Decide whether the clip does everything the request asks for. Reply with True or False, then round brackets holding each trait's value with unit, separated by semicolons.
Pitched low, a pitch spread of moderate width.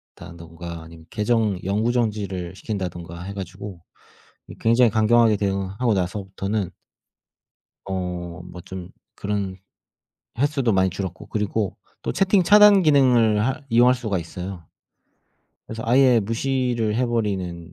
True (105 Hz; 4.4 semitones)